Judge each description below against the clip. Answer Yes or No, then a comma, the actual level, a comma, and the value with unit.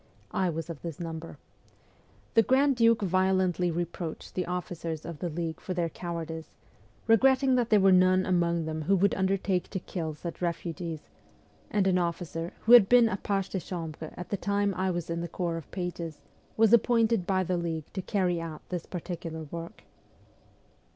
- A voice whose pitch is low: No, medium, 180 Hz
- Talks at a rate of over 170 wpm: Yes, average, 180 wpm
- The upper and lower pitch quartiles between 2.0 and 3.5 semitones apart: Yes, average, 2.7 semitones